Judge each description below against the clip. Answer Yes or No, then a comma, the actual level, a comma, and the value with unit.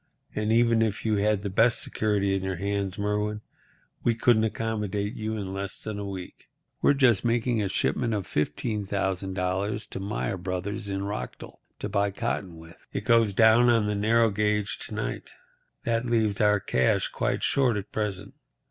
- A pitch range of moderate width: No, narrow, 2.2 semitones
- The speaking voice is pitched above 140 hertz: No, low, 105 Hz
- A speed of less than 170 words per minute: No, average, 175 wpm